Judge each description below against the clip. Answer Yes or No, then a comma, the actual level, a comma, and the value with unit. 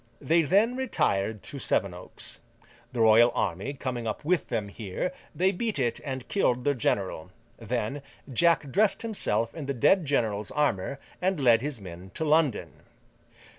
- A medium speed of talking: Yes, average, 155 wpm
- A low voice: Yes, low, 130 Hz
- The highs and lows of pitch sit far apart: Yes, wide, 6.9 semitones